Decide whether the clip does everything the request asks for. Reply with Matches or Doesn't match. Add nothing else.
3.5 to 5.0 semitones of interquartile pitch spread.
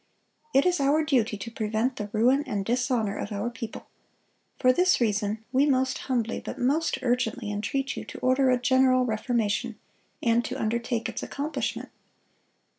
Doesn't match